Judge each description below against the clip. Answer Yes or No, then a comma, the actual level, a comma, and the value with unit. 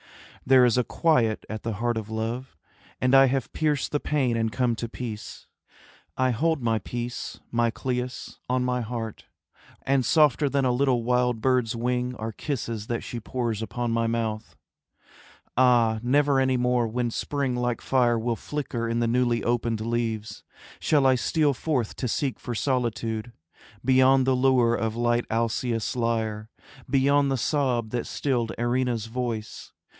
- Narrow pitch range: Yes, narrow, 2.1 semitones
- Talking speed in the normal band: Yes, average, 160 wpm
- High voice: No, low, 120 Hz